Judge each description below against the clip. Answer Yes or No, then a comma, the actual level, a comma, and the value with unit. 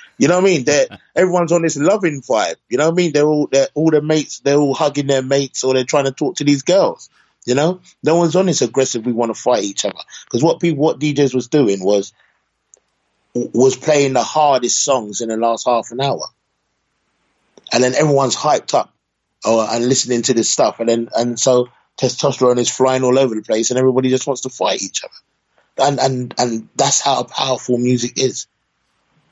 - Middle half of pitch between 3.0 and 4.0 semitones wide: Yes, average, 3.5 semitones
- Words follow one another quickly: Yes, fast, 215 wpm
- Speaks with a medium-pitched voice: No, low, 130 Hz